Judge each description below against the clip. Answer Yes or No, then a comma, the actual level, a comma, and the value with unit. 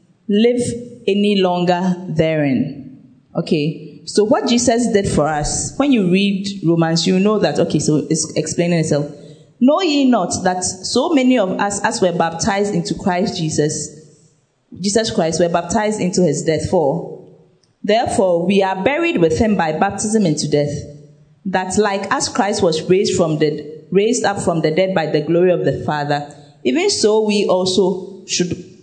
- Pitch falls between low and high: Yes, medium, 180 Hz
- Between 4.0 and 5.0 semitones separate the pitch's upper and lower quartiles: Yes, average, 4.7 semitones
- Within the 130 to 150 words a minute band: No, average, 165 wpm